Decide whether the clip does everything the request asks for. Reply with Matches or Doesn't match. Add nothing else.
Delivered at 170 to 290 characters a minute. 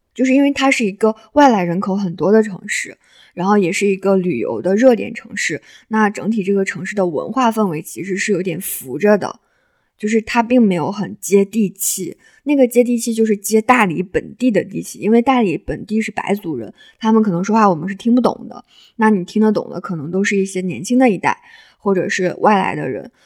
Doesn't match